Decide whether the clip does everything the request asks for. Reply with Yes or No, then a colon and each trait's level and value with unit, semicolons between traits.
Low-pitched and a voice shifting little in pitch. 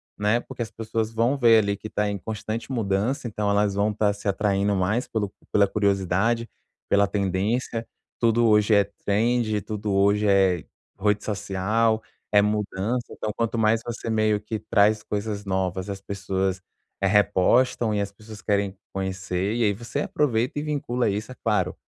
Yes: low, 105 Hz; narrow, 2.2 semitones